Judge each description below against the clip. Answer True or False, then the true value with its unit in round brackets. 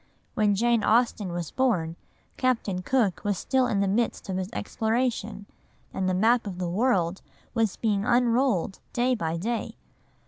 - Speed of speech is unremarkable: True (160 wpm)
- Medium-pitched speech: False (215 Hz)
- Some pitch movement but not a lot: True (4.3 semitones)